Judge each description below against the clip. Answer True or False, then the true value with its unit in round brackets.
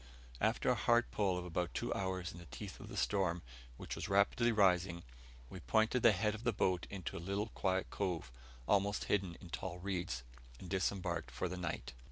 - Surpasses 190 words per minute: True (200 wpm)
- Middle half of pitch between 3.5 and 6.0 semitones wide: False (2.7 semitones)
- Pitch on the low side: True (95 Hz)